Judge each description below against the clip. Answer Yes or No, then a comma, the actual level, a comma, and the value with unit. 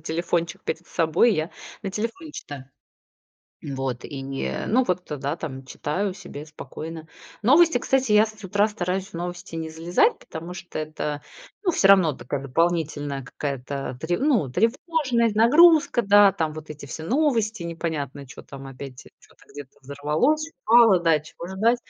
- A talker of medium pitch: Yes, medium, 170 Hz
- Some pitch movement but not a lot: No, wide, 6.7 semitones